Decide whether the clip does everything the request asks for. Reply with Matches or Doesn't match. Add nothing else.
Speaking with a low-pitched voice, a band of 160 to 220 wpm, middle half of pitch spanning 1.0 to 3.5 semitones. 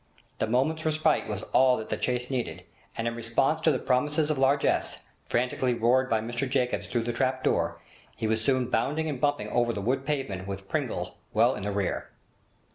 Matches